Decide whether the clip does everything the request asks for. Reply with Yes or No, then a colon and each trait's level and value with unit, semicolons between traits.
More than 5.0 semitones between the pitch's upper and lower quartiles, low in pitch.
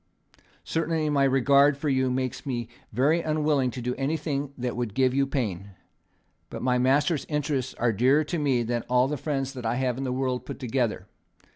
No: average, 2.7 semitones; low, 130 Hz